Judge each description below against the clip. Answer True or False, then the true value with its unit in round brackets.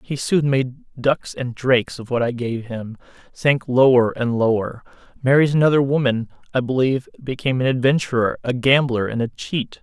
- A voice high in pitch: False (130 Hz)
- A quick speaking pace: False (170 wpm)